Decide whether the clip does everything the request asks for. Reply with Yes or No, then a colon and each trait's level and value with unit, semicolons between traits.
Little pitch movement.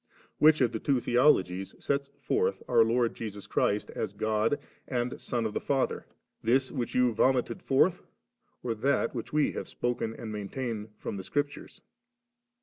No: average, 3.7 semitones